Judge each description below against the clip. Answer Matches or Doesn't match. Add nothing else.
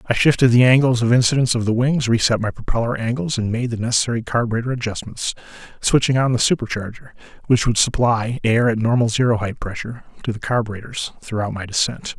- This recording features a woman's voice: Doesn't match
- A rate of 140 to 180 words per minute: Doesn't match